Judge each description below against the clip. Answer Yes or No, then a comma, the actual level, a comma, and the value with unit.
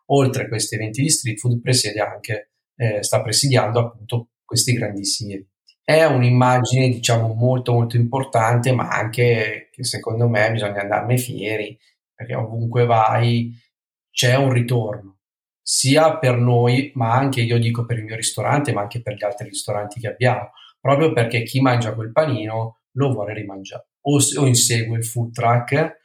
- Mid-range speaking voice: No, low, 120 Hz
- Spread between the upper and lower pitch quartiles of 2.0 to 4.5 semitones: Yes, narrow, 2.5 semitones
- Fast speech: No, average, 160 wpm